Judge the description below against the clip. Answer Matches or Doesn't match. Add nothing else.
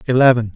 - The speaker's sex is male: Matches